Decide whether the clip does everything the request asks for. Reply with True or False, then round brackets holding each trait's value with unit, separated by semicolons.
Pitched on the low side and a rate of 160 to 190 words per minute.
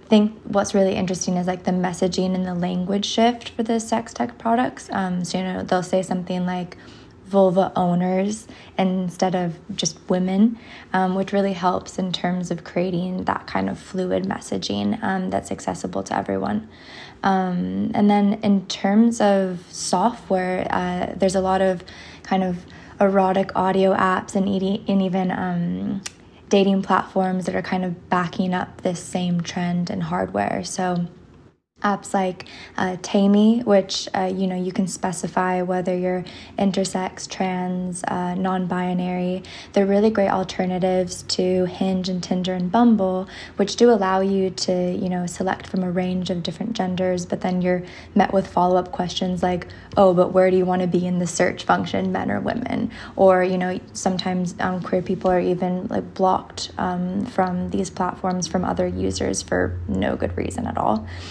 False (185 Hz; 170 wpm)